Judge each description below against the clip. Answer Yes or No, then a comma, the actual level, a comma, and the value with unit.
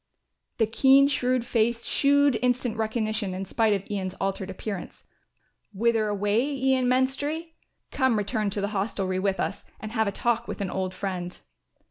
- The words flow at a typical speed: Yes, average, 160 wpm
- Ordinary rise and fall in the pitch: Yes, average, 4.1 semitones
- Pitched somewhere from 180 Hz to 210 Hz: No, high, 220 Hz